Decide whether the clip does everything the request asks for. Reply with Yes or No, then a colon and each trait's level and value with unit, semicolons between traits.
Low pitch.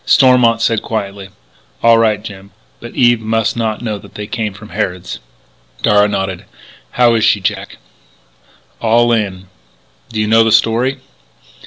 Yes: low, 110 Hz